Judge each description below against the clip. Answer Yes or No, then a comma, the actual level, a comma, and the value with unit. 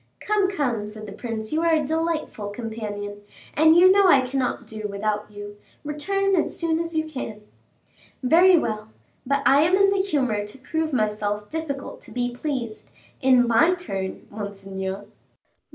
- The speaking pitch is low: No, very high, 255 Hz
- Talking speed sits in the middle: Yes, average, 165 wpm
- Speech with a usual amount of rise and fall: No, wide, 7.4 semitones